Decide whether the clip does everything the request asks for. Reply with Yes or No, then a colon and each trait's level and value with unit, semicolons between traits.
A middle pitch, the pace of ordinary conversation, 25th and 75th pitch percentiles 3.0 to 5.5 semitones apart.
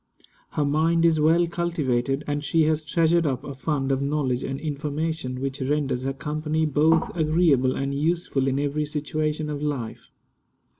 No: medium, 150 Hz; average, 160 wpm; narrow, 2.6 semitones